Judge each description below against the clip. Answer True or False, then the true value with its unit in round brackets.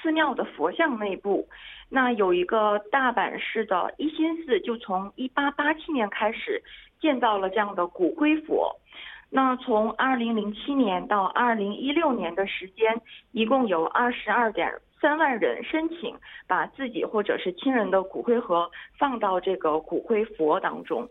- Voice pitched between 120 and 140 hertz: False (240 Hz)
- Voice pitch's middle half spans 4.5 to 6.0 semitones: False (6.4 semitones)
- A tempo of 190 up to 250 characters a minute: True (240 characters per minute)